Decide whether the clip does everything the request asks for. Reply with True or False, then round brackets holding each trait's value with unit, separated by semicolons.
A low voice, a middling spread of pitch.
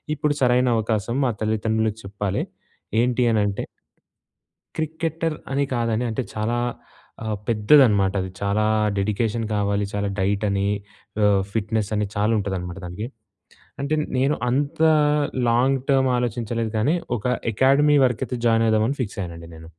True (110 Hz; 3.8 semitones)